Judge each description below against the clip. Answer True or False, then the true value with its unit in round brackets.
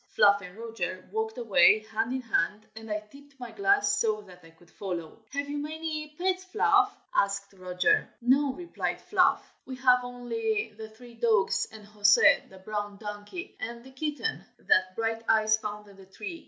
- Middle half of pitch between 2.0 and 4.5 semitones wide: False (5.3 semitones)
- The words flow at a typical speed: True (175 wpm)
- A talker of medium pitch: False (225 Hz)